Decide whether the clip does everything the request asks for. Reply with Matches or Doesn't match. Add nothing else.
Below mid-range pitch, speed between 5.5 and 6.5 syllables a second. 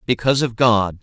Matches